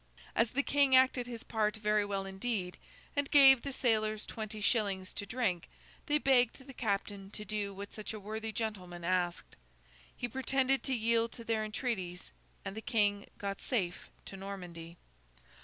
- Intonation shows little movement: No, average, 3.7 semitones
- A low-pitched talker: No, high, 215 Hz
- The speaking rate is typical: Yes, average, 165 wpm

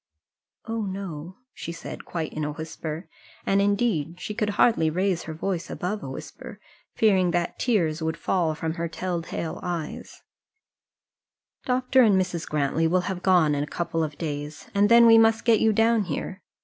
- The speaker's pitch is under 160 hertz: No, medium, 180 Hz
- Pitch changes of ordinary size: Yes, average, 4.3 semitones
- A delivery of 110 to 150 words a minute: No, average, 175 wpm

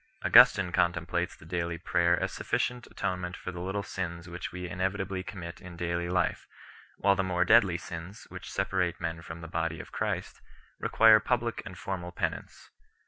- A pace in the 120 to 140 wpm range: No, average, 175 wpm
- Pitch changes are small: Yes, narrow, 2.0 semitones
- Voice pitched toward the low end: Yes, very low, 90 Hz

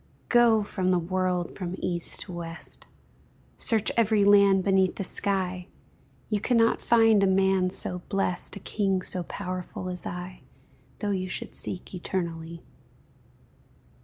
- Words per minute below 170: Yes, slow, 135 wpm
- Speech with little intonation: Yes, narrow, 2.0 semitones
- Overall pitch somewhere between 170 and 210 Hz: Yes, medium, 185 Hz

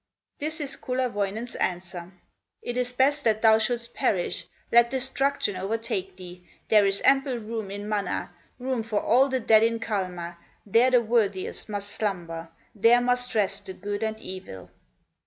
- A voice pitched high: Yes, high, 220 Hz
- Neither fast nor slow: Yes, average, 155 wpm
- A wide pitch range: No, average, 4.1 semitones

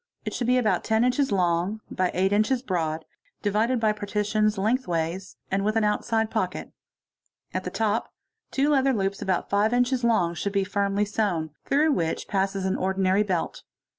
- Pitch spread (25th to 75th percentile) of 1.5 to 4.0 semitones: Yes, average, 3.0 semitones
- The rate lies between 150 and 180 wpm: Yes, average, 170 wpm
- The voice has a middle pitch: No, high, 205 Hz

